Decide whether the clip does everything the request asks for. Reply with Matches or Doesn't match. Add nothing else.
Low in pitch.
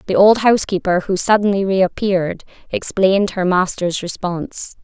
Doesn't match